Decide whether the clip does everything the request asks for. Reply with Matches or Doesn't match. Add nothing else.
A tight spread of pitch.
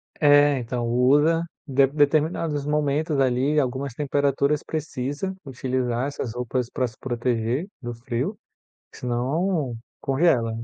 Doesn't match